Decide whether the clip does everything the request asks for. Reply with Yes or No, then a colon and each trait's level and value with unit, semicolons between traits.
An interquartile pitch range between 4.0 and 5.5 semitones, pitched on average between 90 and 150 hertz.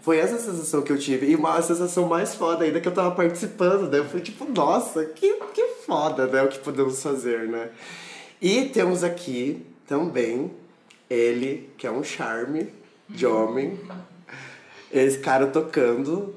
No: average, 5.1 semitones; medium, 160 Hz